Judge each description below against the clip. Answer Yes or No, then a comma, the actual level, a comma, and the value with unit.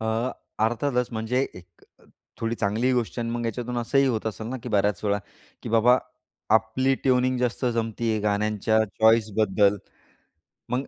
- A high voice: No, low, 115 Hz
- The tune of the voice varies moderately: No, narrow, 2.3 semitones